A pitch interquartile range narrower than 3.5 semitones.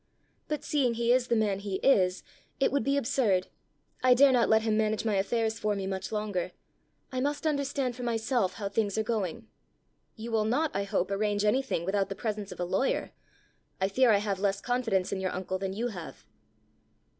No: average, 3.9 semitones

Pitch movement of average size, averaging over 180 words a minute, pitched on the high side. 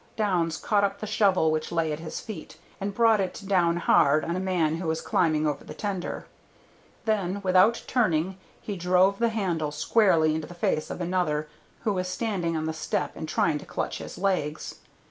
No: average, 3.9 semitones; average, 195 wpm; medium, 180 Hz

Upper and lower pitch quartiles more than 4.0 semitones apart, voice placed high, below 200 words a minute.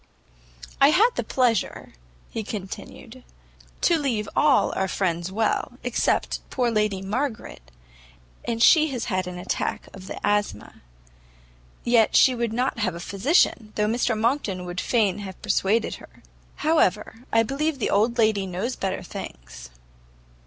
Yes: average, 4.5 semitones; high, 215 Hz; average, 145 wpm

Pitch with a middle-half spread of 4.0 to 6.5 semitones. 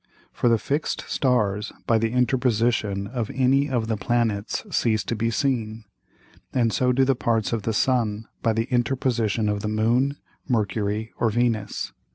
No: narrow, 2.5 semitones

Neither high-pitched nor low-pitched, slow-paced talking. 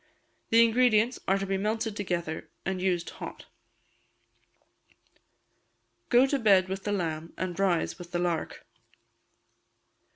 No: high, 195 Hz; slow, 125 wpm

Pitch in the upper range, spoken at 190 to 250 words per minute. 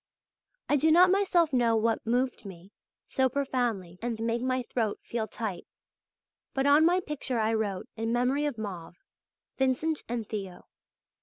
No: high, 240 Hz; average, 155 wpm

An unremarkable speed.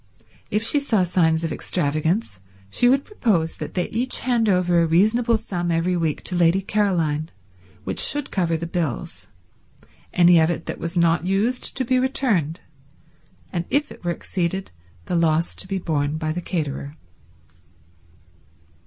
Yes: average, 160 wpm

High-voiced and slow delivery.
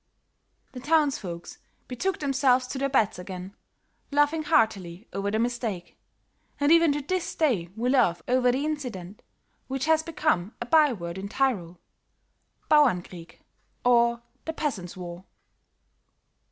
Yes: high, 245 Hz; slow, 130 wpm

